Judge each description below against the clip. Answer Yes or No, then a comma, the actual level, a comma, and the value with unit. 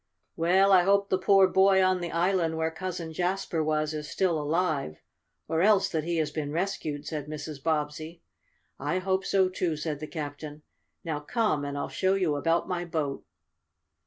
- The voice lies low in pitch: No, medium, 165 Hz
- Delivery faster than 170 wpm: Yes, average, 180 wpm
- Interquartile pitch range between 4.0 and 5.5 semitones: No, average, 3.5 semitones